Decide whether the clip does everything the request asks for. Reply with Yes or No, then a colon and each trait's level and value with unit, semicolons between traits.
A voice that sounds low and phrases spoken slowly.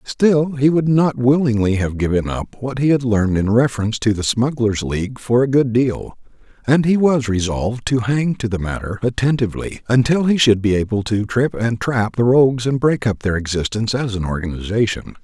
No: low, 120 Hz; average, 200 wpm